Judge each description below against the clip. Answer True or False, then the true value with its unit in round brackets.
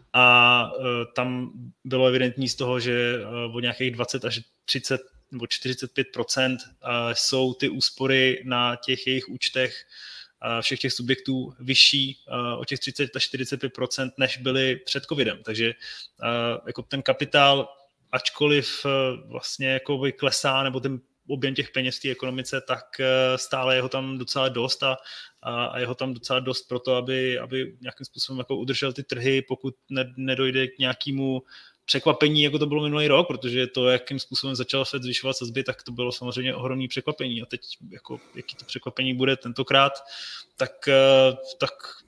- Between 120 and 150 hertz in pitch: True (130 Hz)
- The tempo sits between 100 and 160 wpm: False (170 wpm)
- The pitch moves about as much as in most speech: False (1.2 semitones)